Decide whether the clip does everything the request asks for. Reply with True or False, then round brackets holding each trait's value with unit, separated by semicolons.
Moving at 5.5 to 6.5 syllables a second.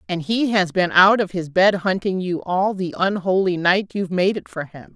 False (4.9 syllables/s)